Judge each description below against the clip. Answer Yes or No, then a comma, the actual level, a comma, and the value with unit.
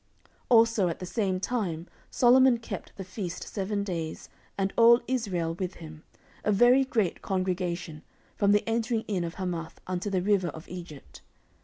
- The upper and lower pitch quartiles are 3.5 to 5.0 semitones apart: Yes, average, 4.4 semitones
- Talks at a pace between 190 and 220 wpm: No, average, 165 wpm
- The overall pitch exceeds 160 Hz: Yes, high, 190 Hz